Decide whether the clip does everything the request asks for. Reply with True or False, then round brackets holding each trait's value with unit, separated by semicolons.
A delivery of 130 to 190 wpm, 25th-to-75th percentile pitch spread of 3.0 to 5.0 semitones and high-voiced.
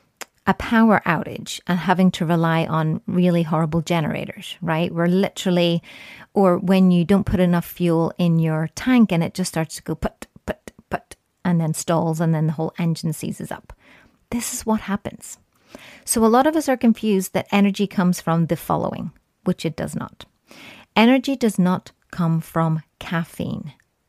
False (175 wpm; 3.4 semitones; 175 Hz)